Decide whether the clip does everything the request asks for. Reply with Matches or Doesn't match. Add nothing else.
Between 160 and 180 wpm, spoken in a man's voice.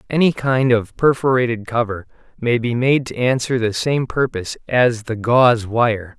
Matches